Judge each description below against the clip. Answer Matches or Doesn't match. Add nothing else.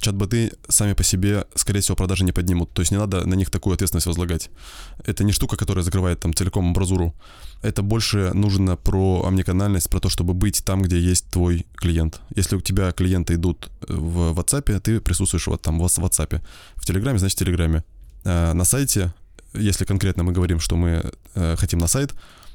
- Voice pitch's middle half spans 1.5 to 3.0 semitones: Matches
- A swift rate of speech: Matches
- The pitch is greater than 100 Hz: Doesn't match